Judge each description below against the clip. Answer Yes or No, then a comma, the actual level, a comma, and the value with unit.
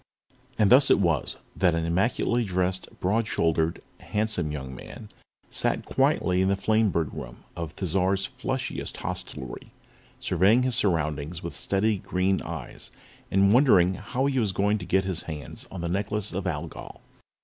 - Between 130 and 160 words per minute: Yes, average, 155 wpm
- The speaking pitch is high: No, very low, 95 Hz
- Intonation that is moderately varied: Yes, average, 4.2 semitones